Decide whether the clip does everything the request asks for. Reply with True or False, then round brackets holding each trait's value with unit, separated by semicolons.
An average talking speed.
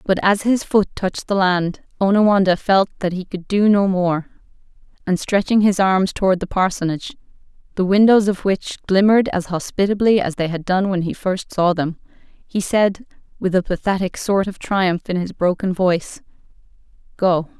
True (175 wpm)